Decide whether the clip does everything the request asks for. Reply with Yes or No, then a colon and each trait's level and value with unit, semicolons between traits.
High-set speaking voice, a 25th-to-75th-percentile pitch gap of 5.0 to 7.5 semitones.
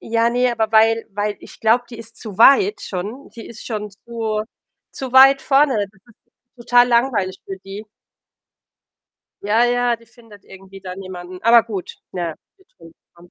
No: high, 225 Hz; average, 3.6 semitones